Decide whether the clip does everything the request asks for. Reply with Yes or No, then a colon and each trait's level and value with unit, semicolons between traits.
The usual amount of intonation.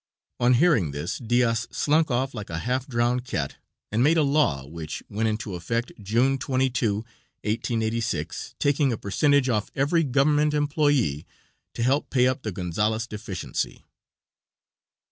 Yes: average, 4.3 semitones